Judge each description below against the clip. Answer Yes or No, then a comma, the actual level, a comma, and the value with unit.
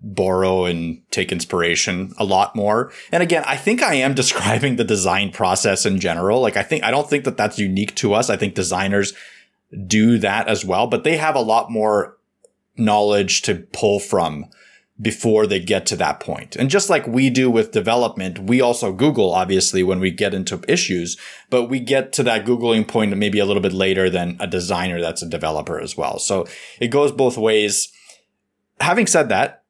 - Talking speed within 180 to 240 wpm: Yes, average, 195 wpm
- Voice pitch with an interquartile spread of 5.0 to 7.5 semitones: Yes, wide, 5.5 semitones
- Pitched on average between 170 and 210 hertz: No, low, 105 Hz